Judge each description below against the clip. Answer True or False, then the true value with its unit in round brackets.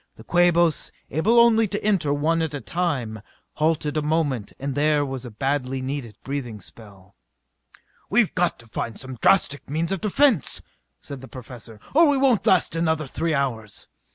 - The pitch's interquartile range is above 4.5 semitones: True (5.2 semitones)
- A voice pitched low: False (145 Hz)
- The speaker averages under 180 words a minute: True (170 wpm)